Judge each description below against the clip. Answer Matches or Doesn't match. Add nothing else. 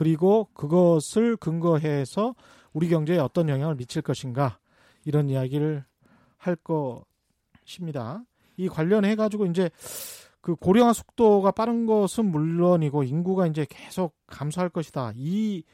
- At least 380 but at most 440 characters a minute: Doesn't match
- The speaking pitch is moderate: Matches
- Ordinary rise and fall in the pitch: Matches